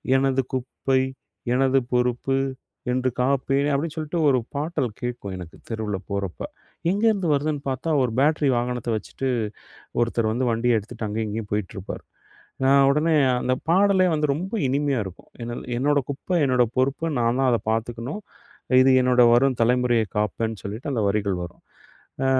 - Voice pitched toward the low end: Yes, low, 125 Hz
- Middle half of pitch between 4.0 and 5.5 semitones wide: No, average, 3.5 semitones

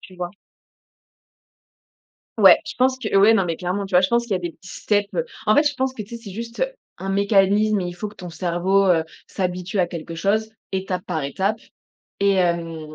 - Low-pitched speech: No, high, 195 Hz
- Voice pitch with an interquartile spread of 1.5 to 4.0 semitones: Yes, average, 3.2 semitones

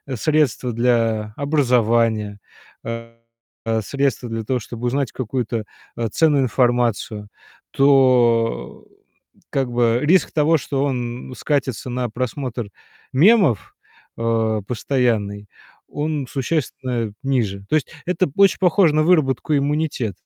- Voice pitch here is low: Yes, low, 125 Hz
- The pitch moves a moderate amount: Yes, average, 3.8 semitones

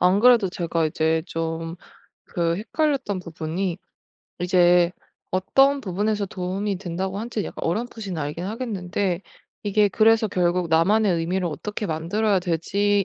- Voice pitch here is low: No, medium, 185 Hz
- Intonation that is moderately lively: Yes, average, 3.6 semitones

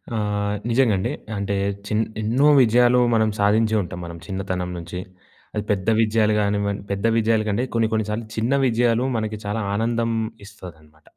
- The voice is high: No, low, 105 Hz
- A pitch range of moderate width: No, narrow, 2.2 semitones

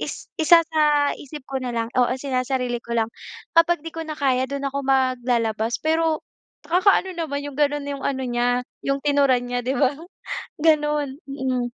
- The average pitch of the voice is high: Yes, very high, 275 Hz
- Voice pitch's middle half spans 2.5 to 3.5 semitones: Yes, average, 3.1 semitones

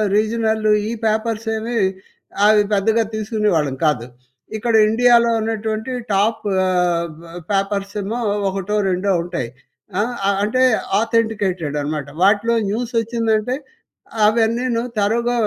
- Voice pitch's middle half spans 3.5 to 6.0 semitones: No, average, 2.7 semitones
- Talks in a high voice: Yes, high, 215 Hz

